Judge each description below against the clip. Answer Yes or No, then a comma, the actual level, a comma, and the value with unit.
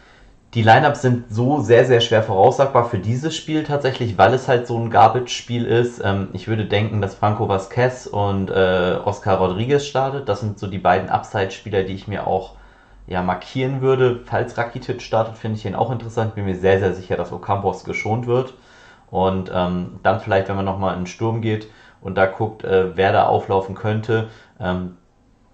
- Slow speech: No, fast, 190 wpm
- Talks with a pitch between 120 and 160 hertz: No, low, 110 Hz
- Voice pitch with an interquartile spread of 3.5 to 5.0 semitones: Yes, average, 3.9 semitones